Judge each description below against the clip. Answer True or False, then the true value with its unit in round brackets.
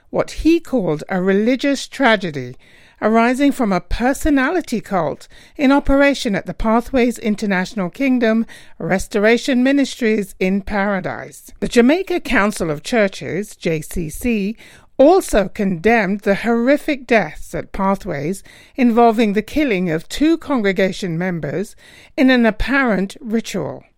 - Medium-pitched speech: False (220 Hz)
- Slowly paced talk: True (115 wpm)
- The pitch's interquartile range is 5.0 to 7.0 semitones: True (5.3 semitones)